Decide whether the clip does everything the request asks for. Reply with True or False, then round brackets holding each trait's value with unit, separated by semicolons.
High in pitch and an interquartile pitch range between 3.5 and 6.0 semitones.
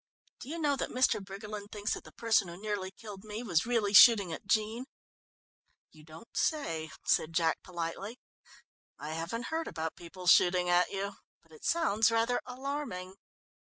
True (205 Hz; 4.6 semitones)